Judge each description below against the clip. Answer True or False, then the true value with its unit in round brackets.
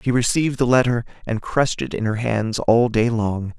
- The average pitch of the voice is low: True (115 Hz)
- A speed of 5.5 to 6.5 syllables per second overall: False (5.3 syllables/s)